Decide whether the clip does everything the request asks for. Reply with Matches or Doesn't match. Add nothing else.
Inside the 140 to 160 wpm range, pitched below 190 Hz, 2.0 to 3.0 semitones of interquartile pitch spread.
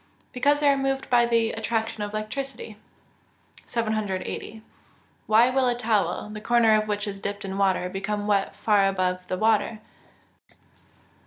Doesn't match